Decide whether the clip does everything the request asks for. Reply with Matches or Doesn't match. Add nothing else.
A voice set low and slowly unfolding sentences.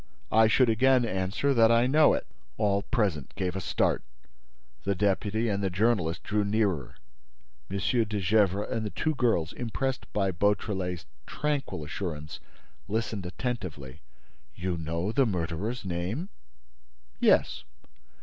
Matches